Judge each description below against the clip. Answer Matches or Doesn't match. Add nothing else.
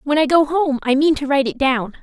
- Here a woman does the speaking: Matches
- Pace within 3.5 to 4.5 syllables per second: Doesn't match